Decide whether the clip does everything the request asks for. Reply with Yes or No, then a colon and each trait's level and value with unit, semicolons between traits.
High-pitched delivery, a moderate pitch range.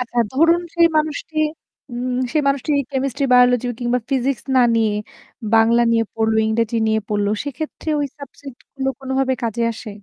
Yes: very high, 250 Hz; average, 3.3 semitones